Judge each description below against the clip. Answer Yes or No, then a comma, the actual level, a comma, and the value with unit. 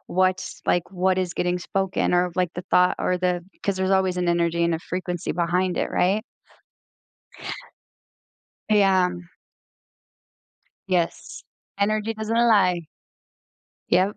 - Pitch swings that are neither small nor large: No, narrow, 1.5 semitones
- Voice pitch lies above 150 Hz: Yes, medium, 185 Hz